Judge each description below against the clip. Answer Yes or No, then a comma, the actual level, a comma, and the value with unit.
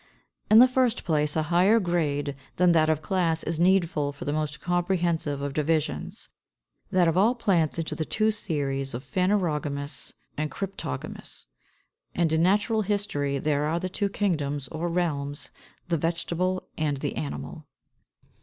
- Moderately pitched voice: Yes, medium, 165 Hz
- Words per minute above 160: No, average, 155 wpm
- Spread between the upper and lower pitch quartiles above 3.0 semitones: Yes, average, 4.1 semitones